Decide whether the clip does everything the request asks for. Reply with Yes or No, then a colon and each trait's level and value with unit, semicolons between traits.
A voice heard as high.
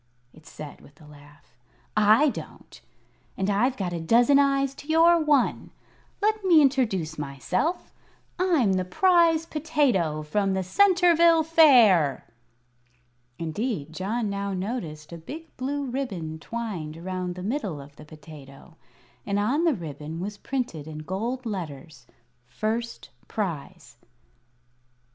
Yes: high, 205 Hz